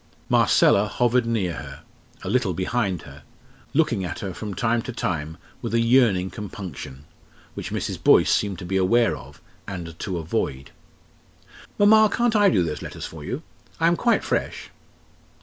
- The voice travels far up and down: Yes, wide, 6.1 semitones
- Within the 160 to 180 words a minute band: Yes, average, 165 wpm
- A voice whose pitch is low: Yes, low, 100 Hz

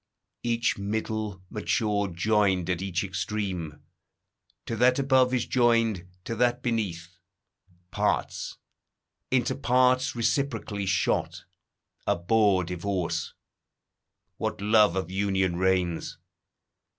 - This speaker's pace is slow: Yes, slow, 95 wpm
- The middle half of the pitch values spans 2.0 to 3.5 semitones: No, average, 4.0 semitones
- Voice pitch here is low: Yes, low, 100 Hz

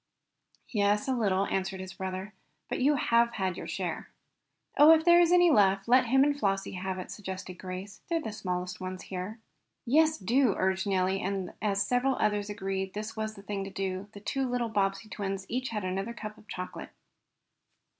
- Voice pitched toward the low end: No, high, 200 Hz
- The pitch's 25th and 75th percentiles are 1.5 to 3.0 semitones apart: No, average, 3.7 semitones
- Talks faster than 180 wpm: Yes, average, 195 wpm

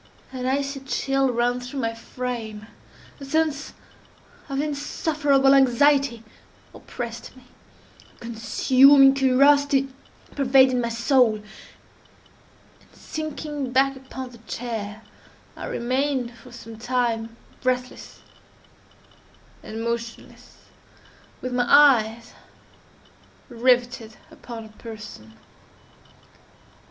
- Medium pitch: No, very high, 250 Hz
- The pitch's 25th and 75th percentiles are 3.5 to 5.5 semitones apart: No, average, 2.7 semitones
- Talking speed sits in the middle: No, slow, 90 wpm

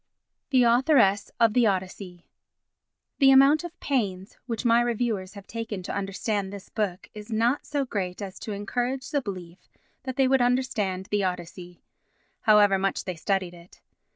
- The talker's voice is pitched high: Yes, high, 210 Hz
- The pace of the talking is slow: No, average, 160 wpm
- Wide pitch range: No, average, 4.5 semitones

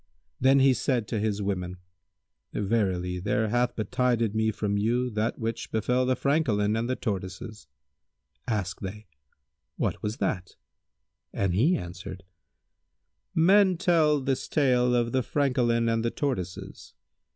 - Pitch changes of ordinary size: Yes, average, 3.9 semitones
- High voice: No, low, 115 Hz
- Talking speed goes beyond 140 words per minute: No, slow, 135 wpm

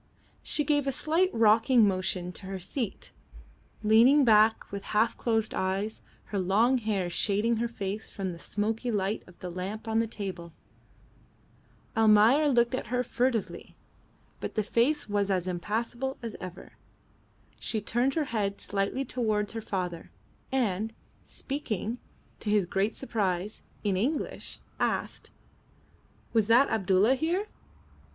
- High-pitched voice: Yes, high, 220 Hz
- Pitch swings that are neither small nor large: Yes, average, 3.5 semitones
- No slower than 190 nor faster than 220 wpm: No, average, 140 wpm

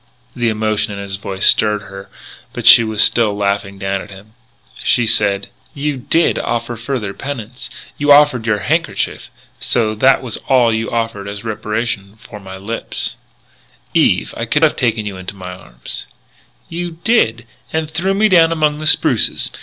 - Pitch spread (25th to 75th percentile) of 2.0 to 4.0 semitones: No, average, 4.6 semitones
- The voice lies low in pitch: Yes, low, 110 Hz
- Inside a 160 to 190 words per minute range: Yes, average, 175 wpm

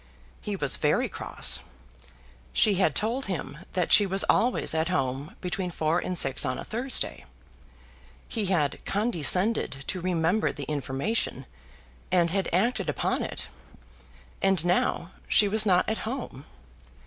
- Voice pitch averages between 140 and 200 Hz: Yes, medium, 185 Hz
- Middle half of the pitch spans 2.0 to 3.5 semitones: No, average, 4.7 semitones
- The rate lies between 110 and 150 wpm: Yes, average, 140 wpm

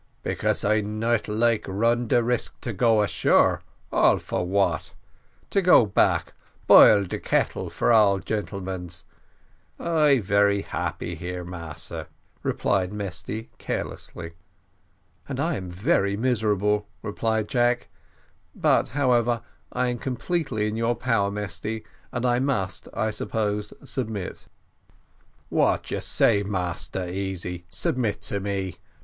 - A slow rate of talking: Yes, slow, 125 wpm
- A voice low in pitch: Yes, low, 105 Hz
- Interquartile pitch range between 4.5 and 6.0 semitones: No, average, 3.5 semitones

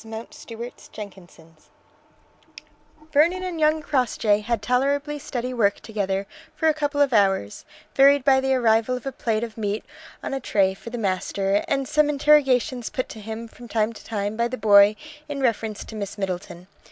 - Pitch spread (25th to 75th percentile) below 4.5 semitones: No, average, 4.8 semitones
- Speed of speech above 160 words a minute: Yes, average, 175 wpm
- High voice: Yes, high, 230 Hz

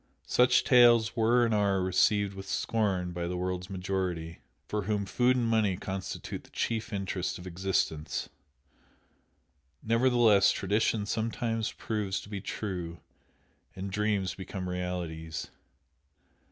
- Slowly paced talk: Yes, slow, 125 wpm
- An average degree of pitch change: Yes, average, 3.4 semitones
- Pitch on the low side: Yes, low, 100 Hz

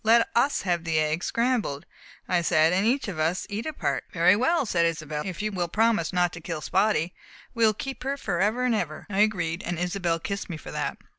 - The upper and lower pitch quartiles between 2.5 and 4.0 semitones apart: No, average, 4.9 semitones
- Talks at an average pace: No, fast, 220 wpm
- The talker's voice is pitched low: No, medium, 185 Hz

